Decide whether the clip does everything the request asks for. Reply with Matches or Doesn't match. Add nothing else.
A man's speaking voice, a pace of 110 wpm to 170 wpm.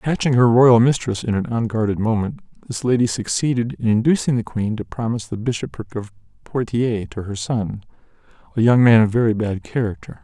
Doesn't match